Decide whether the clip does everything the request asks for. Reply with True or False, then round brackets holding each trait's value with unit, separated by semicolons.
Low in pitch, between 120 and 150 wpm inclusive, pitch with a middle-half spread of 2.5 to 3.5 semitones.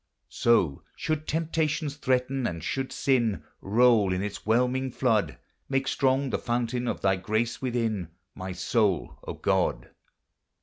False (120 Hz; 135 wpm; 4.3 semitones)